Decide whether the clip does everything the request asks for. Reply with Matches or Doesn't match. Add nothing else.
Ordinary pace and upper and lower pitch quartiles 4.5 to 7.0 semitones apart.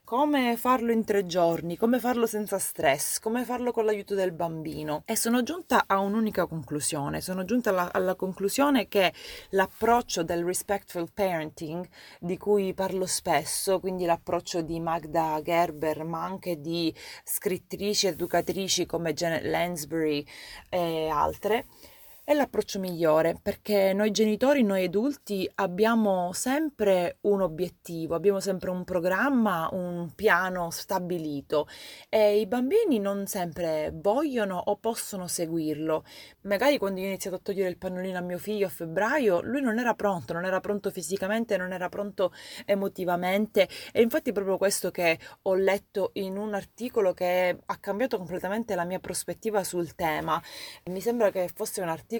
Doesn't match